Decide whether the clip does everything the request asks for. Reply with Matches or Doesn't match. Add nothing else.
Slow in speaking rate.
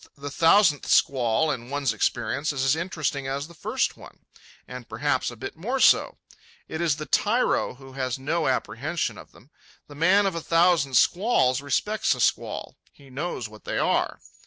Doesn't match